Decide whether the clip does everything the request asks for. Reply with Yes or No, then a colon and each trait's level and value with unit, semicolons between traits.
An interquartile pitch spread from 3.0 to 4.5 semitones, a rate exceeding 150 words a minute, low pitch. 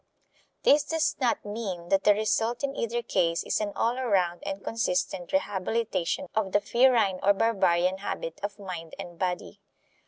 No: average, 4.0 semitones; average, 160 wpm; high, 205 Hz